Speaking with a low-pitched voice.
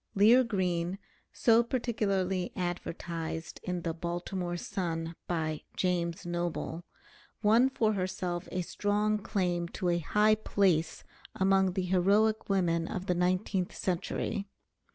No: medium, 185 Hz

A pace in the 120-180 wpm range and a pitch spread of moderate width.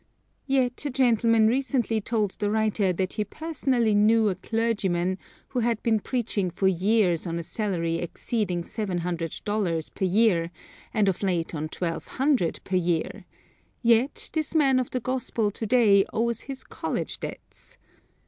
Yes: average, 160 wpm; average, 4.5 semitones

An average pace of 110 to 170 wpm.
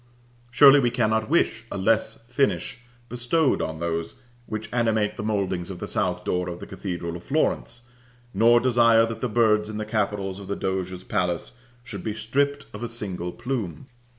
No: average, 180 wpm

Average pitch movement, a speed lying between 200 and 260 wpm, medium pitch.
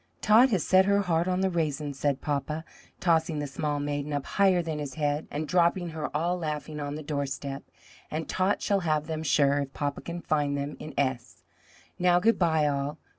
Yes: average, 3.2 semitones; fast, 205 wpm; medium, 155 Hz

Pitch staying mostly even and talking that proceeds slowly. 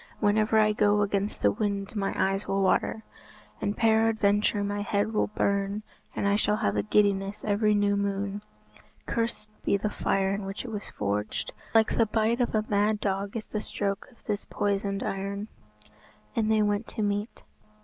No: narrow, 1.2 semitones; average, 180 wpm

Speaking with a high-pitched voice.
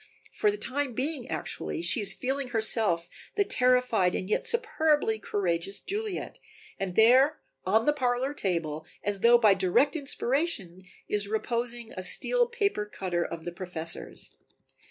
Yes: high, 235 Hz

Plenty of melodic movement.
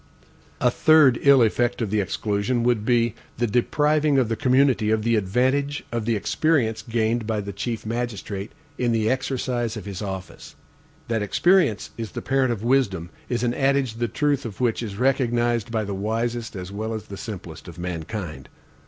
No: average, 3.2 semitones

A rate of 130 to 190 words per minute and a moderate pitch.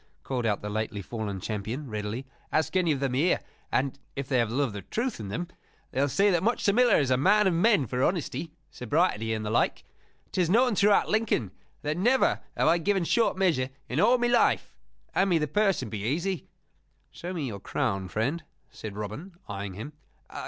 No: fast, 205 wpm; medium, 145 Hz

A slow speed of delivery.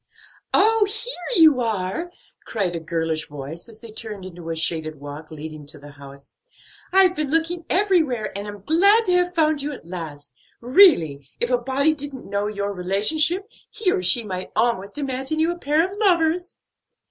No: average, 180 wpm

